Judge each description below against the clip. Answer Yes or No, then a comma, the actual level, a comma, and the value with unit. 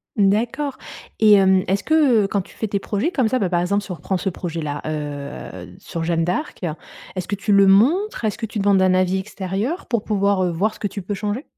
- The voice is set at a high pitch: Yes, high, 200 Hz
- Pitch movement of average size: Yes, average, 3.1 semitones